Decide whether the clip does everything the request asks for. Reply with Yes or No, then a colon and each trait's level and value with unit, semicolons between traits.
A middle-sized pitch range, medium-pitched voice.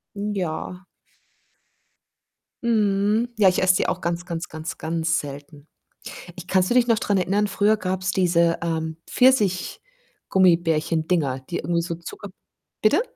Yes: average, 3.6 semitones; medium, 180 Hz